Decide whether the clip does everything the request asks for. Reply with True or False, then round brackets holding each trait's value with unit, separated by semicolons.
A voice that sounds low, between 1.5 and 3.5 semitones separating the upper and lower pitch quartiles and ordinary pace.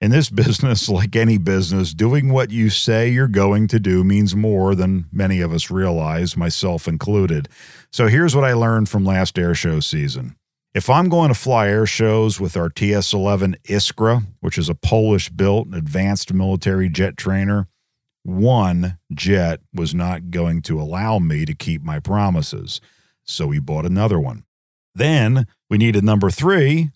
False (100 Hz; 4.2 semitones; 165 wpm)